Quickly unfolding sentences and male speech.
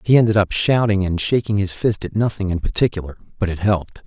Yes: fast, 220 wpm; male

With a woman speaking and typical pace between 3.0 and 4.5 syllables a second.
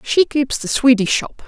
Yes: female; 4.4 syllables/s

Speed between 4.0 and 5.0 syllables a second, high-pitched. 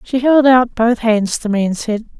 Yes: 4.6 syllables/s; high, 230 Hz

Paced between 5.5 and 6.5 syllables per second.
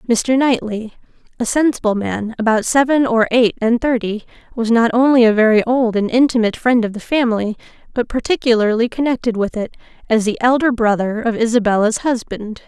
Yes: 5.6 syllables/s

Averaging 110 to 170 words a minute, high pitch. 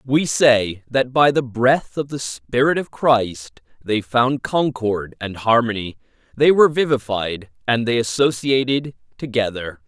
No: average, 140 wpm; low, 120 Hz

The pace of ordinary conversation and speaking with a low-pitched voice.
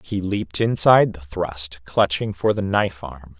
Yes: average, 175 wpm; very low, 90 Hz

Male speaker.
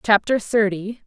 No: female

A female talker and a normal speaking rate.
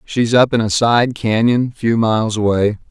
No: male; average, 185 wpm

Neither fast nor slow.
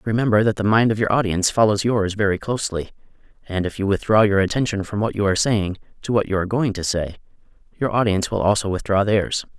No: fast, 220 wpm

